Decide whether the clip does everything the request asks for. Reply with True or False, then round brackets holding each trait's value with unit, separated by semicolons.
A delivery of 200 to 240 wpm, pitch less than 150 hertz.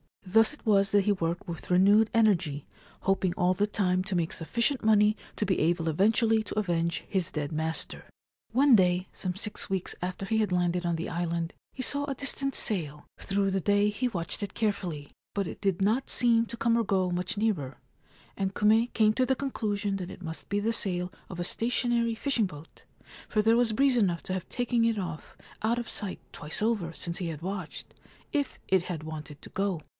False (205 wpm; 195 Hz)